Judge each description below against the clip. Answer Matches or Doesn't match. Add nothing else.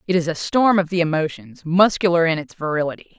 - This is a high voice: Doesn't match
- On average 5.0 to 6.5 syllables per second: Matches